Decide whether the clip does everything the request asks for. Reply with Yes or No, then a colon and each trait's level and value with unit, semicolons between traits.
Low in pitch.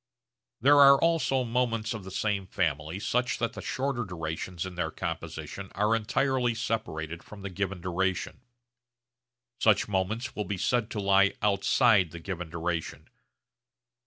Yes: low, 100 Hz